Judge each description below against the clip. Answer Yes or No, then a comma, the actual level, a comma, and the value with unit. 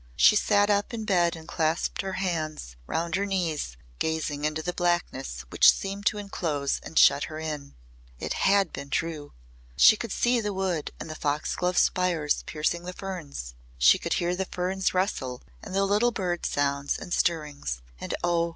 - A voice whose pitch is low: No, medium, 170 Hz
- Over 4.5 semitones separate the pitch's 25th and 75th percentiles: No, average, 4.2 semitones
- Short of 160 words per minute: No, average, 180 wpm